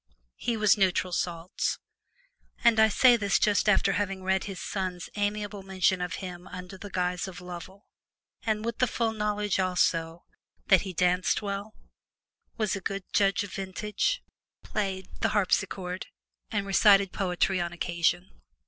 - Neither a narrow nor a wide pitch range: No, narrow, 2.3 semitones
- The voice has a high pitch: Yes, high, 195 Hz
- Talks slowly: No, average, 150 wpm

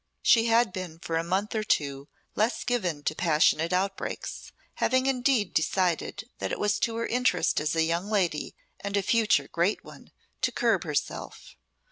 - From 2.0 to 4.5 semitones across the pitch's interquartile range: No, wide, 5.4 semitones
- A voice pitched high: Yes, high, 195 Hz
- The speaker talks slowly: No, average, 170 wpm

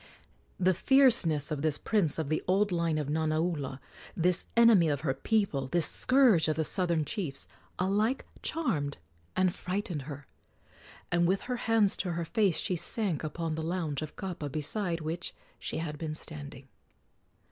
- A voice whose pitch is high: No, medium, 170 Hz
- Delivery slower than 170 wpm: Yes, average, 160 wpm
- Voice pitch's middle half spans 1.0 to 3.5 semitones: No, average, 4.1 semitones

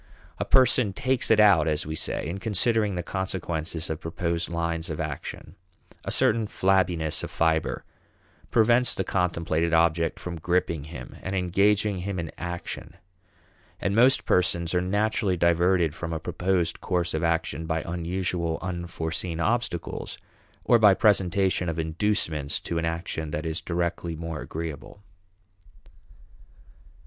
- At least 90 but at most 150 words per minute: Yes, average, 140 wpm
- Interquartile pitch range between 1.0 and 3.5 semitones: Yes, average, 2.8 semitones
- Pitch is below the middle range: Yes, very low, 85 Hz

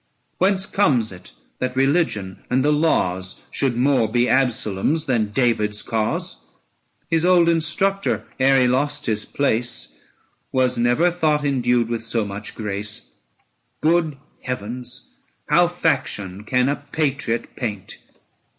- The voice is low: Yes, low, 125 Hz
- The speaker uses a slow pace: Yes, slow, 130 wpm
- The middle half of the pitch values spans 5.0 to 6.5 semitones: Yes, average, 5.3 semitones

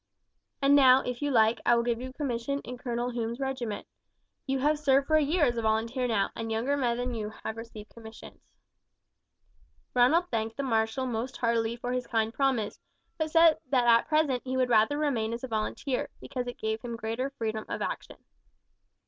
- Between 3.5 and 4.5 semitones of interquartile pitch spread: No, average, 3.0 semitones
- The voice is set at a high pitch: Yes, high, 245 Hz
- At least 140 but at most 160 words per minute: No, average, 200 wpm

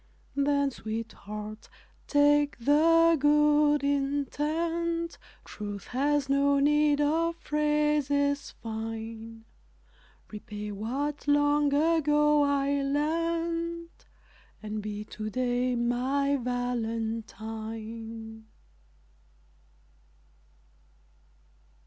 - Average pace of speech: No, slow, 70 wpm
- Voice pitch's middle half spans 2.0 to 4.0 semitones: No, average, 4.8 semitones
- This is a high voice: Yes, very high, 280 Hz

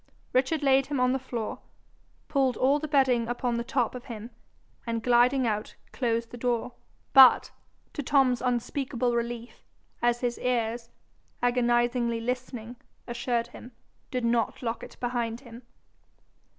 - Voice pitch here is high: Yes, high, 245 Hz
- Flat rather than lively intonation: Yes, narrow, 1.5 semitones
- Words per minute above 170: No, average, 140 wpm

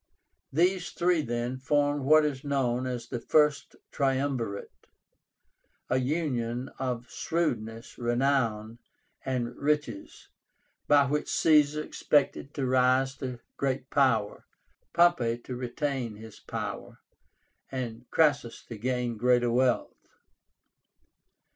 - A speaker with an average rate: No, slow, 105 wpm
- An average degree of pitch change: Yes, average, 3.3 semitones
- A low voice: Yes, low, 130 Hz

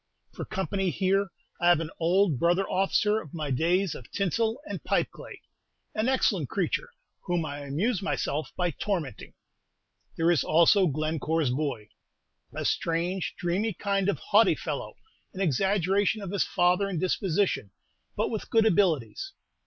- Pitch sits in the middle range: Yes, medium, 180 Hz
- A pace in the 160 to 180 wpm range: No, average, 150 wpm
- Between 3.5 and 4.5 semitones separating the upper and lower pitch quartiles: Yes, average, 3.8 semitones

